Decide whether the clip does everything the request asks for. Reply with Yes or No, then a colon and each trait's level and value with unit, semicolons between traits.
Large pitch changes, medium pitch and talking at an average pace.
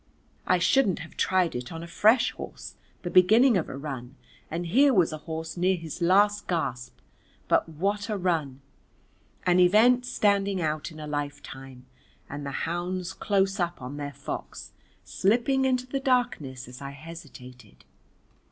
Yes: wide, 5.8 semitones; medium, 175 Hz; average, 160 wpm